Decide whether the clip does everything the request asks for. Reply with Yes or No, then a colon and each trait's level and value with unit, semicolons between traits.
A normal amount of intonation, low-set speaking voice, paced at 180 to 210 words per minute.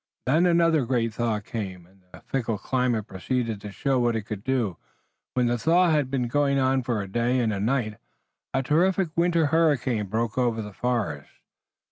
Yes: average, 4.0 semitones; low, 120 Hz; average, 185 wpm